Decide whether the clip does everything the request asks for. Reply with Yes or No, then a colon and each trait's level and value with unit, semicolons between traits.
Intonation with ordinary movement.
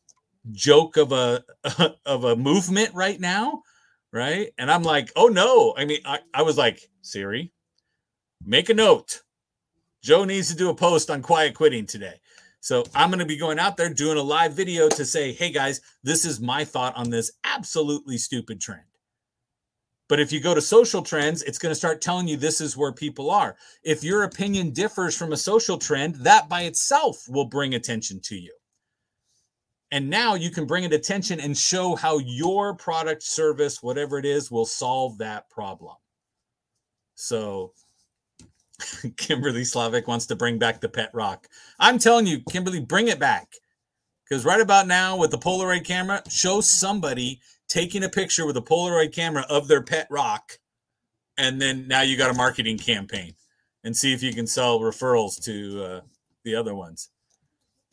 No: wide, 6.5 semitones